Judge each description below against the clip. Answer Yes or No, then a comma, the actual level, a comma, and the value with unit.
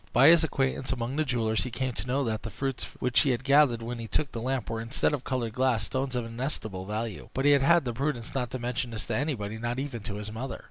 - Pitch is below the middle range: Yes, low, 125 Hz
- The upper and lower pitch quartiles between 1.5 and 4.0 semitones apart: Yes, average, 2.9 semitones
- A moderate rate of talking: No, fast, 265 wpm